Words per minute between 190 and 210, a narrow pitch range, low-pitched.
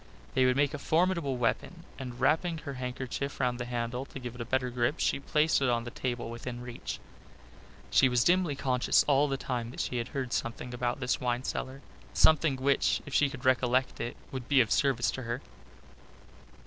Yes: average, 200 wpm; narrow, 2.3 semitones; low, 130 Hz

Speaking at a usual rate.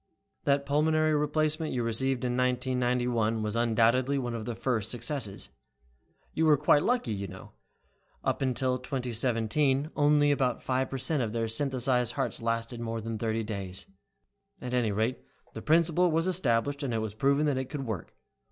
Yes: average, 170 wpm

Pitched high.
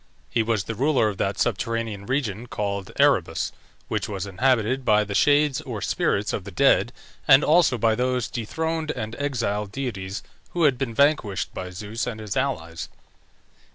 No: low, 115 Hz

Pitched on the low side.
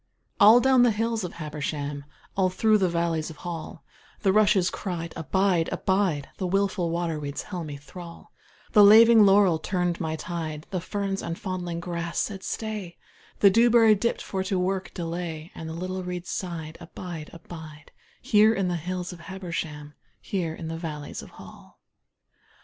No: medium, 180 Hz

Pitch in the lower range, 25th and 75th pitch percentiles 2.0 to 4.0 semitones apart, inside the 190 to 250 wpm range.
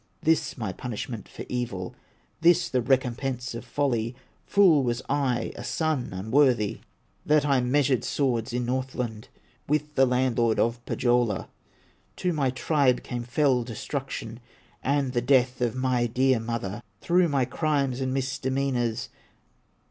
No: low, 125 Hz; narrow, 2.6 semitones; slow, 135 wpm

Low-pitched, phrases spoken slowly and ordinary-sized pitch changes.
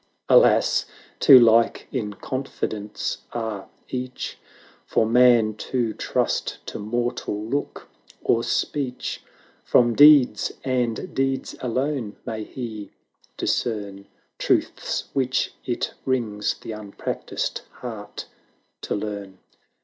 Yes: low, 115 Hz; slow, 100 wpm; average, 3.2 semitones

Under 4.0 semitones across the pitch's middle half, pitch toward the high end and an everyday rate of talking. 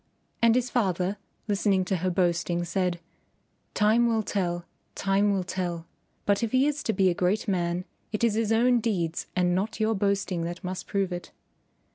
Yes: average, 3.5 semitones; high, 195 Hz; average, 180 wpm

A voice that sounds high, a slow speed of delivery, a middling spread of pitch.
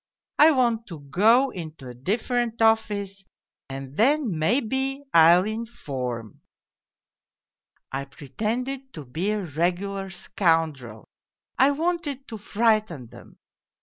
No: high, 200 Hz; slow, 115 wpm; wide, 7.5 semitones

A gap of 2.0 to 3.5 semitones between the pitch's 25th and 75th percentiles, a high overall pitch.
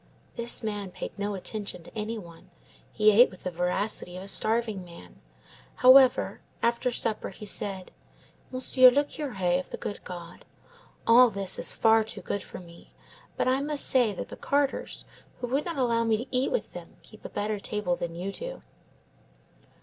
No: average, 5.0 semitones; high, 215 Hz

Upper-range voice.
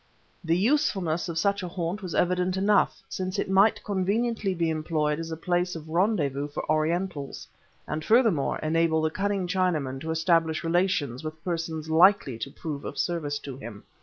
No: medium, 165 Hz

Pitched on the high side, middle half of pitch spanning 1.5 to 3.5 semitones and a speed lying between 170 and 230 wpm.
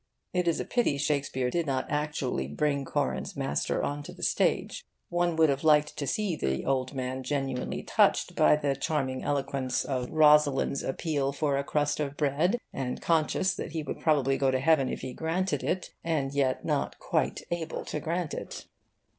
No: medium, 145 Hz; average, 2.9 semitones; average, 185 wpm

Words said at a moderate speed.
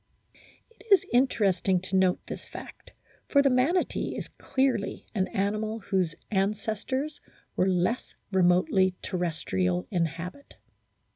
No: slow, 125 wpm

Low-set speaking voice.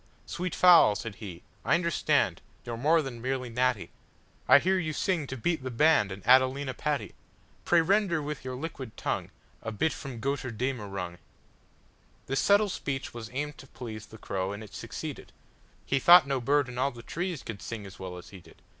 Yes: low, 130 Hz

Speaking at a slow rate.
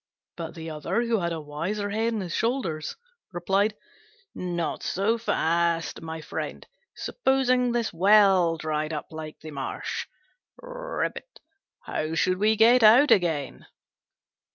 Yes: slow, 130 wpm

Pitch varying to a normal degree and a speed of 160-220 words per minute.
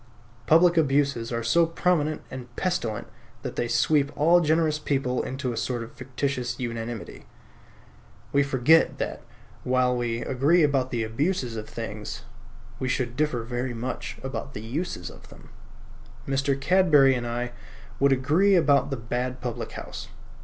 No: average, 3.7 semitones; average, 150 wpm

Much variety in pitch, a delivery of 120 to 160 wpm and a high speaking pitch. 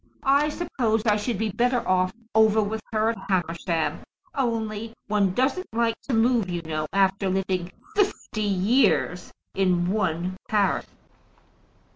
No: average, 3.8 semitones; slow, 135 wpm; high, 210 Hz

